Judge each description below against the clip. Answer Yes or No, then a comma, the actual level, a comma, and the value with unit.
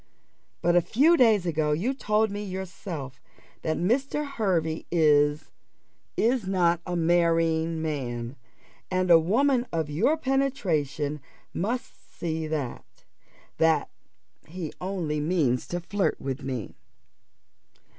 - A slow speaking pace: Yes, slow, 115 wpm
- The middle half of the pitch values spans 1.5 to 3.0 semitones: No, average, 5.0 semitones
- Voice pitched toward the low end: No, medium, 170 Hz